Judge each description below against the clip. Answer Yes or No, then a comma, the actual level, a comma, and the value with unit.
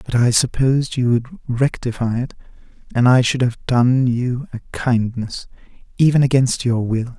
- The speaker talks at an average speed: Yes, average, 160 wpm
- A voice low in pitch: Yes, low, 125 Hz